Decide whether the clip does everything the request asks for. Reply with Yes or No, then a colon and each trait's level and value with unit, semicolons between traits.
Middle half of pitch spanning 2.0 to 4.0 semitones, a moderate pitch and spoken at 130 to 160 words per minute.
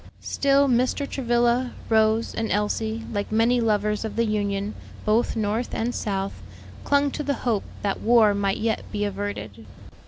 No: average, 2.7 semitones; high, 220 Hz; average, 155 wpm